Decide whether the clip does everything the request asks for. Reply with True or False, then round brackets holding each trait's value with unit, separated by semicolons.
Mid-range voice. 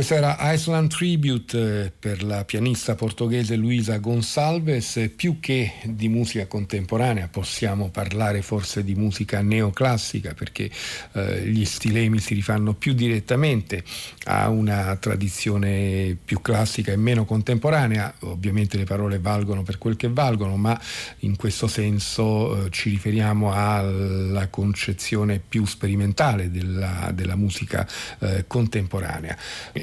False (105 Hz)